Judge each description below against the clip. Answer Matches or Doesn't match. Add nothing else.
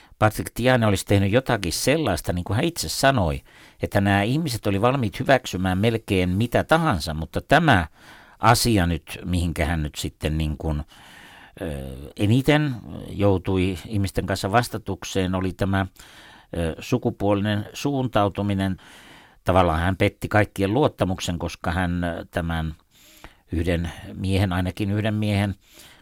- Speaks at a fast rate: Doesn't match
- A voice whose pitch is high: Doesn't match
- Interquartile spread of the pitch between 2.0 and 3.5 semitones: Doesn't match